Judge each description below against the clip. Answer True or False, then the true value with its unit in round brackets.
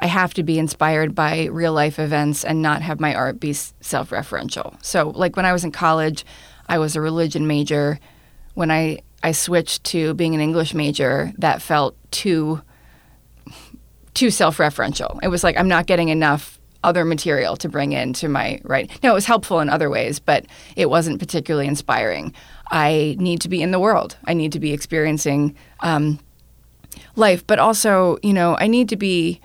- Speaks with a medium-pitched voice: True (160 Hz)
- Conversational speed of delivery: True (185 wpm)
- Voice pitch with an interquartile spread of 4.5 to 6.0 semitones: False (2.6 semitones)